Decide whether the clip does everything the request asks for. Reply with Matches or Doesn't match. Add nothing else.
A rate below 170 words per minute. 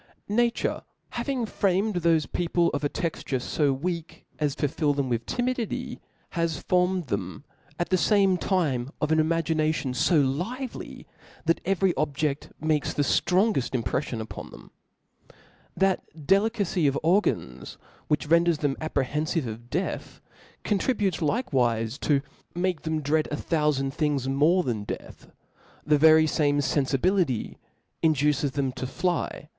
Matches